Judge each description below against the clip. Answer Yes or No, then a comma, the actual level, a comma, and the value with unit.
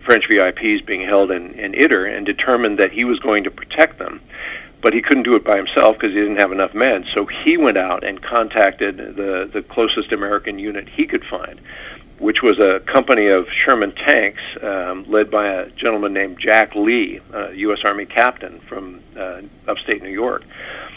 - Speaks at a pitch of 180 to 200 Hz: No, low, 110 Hz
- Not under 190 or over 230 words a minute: Yes, average, 195 wpm